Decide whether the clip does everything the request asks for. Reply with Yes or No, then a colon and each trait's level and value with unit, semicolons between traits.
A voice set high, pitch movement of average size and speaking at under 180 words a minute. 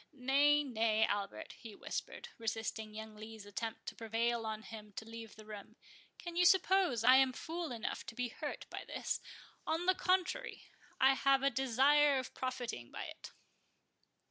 Yes: high, 240 Hz; average, 4.4 semitones; average, 165 wpm